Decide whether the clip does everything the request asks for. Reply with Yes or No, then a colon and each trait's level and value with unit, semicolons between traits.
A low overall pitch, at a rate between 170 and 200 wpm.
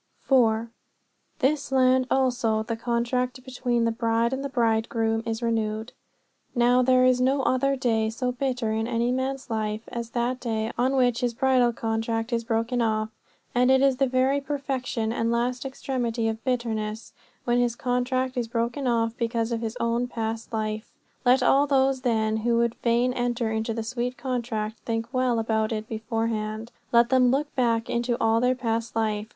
No: high, 235 Hz; average, 180 wpm